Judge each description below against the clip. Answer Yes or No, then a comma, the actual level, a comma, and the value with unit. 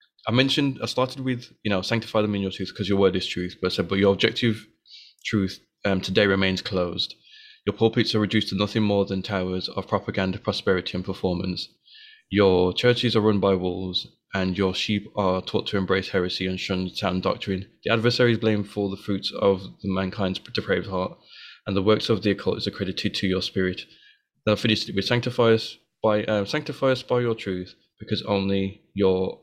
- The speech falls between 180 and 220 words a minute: Yes, average, 200 wpm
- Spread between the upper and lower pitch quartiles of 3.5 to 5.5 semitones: No, average, 2.8 semitones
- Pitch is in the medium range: No, low, 100 Hz